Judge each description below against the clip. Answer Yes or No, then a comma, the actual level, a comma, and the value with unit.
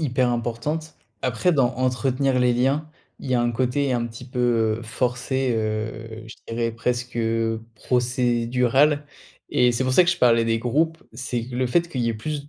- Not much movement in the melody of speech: Yes, narrow, 2.3 semitones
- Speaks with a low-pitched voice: Yes, low, 125 Hz